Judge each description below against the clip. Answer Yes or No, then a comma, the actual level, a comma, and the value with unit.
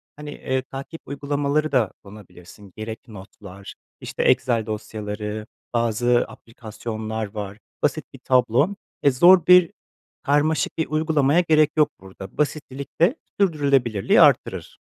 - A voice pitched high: No, low, 125 Hz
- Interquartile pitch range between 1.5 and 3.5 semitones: No, wide, 5.6 semitones